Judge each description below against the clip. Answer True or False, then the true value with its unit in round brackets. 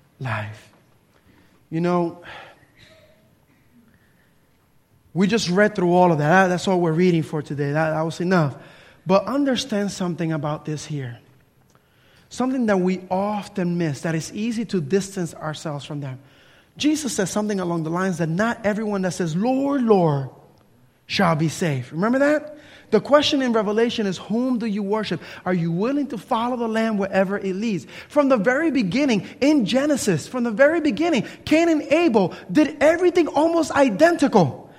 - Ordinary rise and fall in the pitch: False (7.1 semitones)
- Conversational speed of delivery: True (160 wpm)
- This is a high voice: True (195 Hz)